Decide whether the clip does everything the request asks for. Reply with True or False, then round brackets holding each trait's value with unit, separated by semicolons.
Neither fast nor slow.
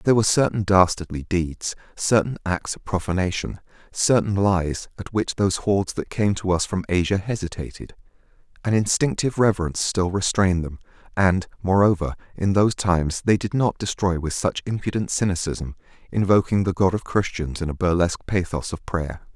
True (160 wpm)